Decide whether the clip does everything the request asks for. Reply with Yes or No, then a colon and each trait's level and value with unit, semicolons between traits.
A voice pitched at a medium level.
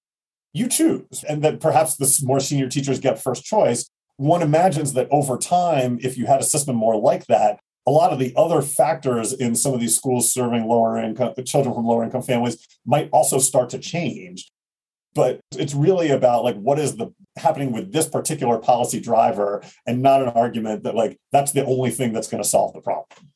No: low, 130 Hz